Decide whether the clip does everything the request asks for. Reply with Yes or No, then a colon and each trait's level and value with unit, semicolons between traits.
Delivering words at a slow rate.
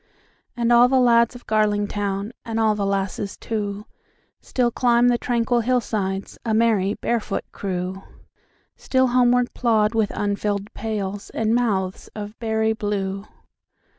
Yes: slow, 110 wpm